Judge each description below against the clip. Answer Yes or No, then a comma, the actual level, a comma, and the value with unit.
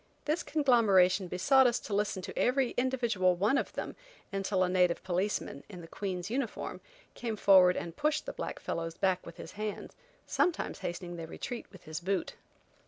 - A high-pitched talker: Yes, high, 195 Hz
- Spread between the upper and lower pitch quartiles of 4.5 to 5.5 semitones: Yes, average, 5.0 semitones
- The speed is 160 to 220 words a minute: Yes, average, 175 wpm